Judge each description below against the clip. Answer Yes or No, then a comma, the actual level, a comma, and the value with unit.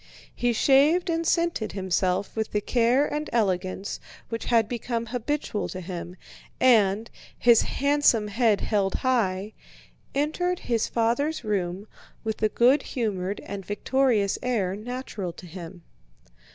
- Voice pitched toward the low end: No, high, 225 Hz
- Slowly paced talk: Yes, slow, 130 wpm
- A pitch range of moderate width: Yes, average, 4.7 semitones